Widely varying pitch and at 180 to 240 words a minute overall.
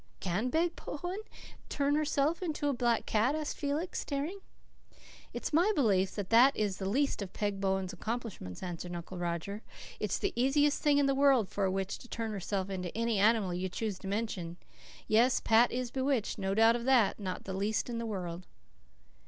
Yes: wide, 6.3 semitones; average, 190 wpm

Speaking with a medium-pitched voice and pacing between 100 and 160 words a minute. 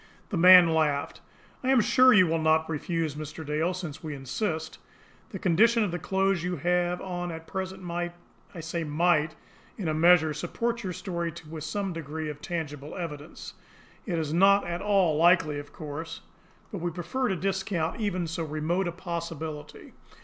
No: medium, 170 Hz; average, 175 wpm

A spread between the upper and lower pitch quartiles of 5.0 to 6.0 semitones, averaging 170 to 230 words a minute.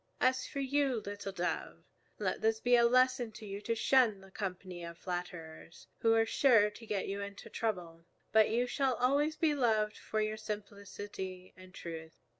No: average, 4.4 semitones; average, 180 wpm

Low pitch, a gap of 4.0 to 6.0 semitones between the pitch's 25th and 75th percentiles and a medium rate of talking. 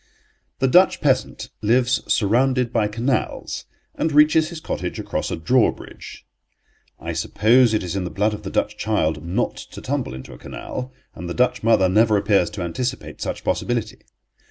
Yes: low, 110 Hz; average, 4.6 semitones; average, 170 wpm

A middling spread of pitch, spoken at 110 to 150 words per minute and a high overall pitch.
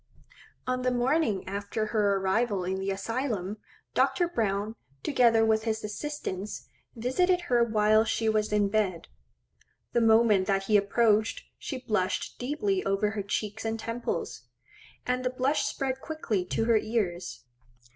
Yes: average, 3.6 semitones; average, 145 wpm; high, 220 Hz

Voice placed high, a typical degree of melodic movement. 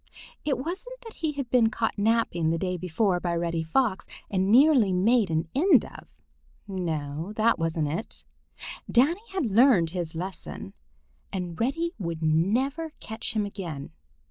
No: high, 200 Hz; wide, 7.3 semitones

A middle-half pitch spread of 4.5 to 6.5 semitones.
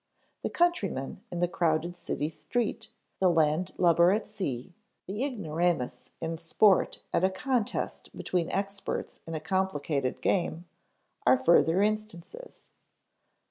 No: average, 3.8 semitones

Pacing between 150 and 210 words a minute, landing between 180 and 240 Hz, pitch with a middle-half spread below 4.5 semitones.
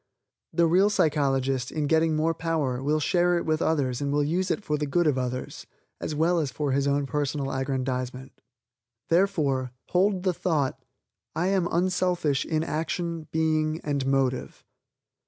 No: average, 160 wpm; medium, 155 Hz; average, 3.7 semitones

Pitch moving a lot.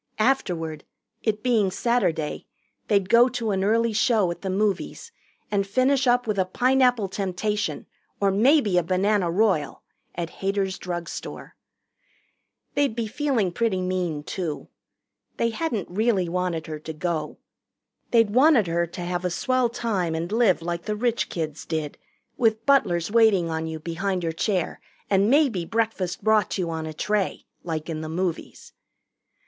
No: average, 4.9 semitones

